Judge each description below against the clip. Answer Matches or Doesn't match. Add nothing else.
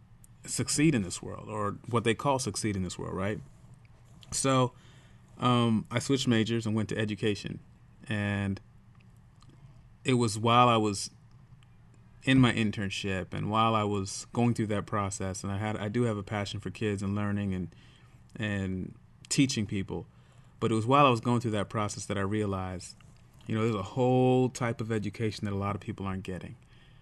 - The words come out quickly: Doesn't match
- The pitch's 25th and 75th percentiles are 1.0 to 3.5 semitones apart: Matches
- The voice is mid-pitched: Doesn't match